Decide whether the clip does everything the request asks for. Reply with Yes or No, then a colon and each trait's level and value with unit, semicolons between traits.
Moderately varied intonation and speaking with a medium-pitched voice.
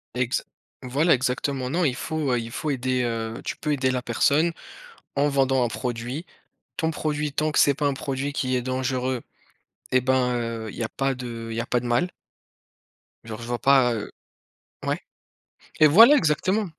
No: average, 3.2 semitones; low, 130 Hz